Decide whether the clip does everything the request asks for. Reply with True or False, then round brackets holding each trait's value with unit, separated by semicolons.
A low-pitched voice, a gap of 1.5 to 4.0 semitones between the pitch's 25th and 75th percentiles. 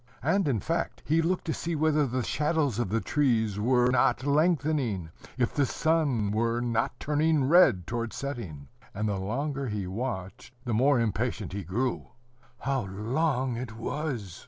False (125 Hz; 5.3 semitones)